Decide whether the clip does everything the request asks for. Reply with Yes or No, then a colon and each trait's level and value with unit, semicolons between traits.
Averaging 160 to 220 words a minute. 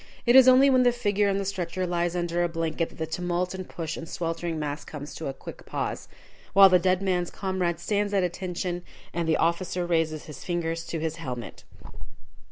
Yes: fast, 205 wpm